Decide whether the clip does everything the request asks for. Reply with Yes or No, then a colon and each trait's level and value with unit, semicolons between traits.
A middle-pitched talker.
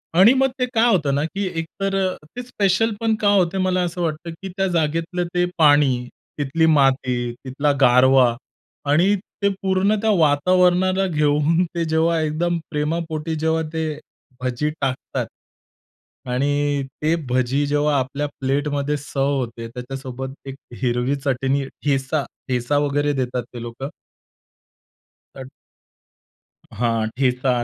Yes: medium, 150 Hz